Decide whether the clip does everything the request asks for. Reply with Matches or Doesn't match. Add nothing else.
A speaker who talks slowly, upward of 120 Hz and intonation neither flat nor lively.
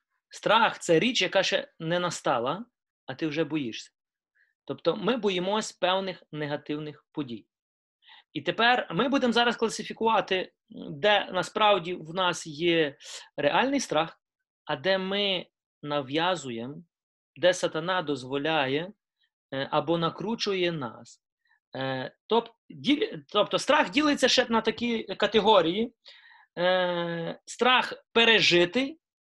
Doesn't match